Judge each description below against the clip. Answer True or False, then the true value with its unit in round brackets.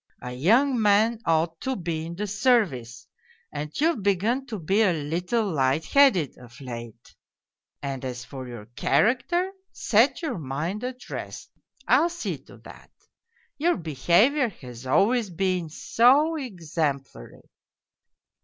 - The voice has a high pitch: False (180 Hz)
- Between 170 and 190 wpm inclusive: False (135 wpm)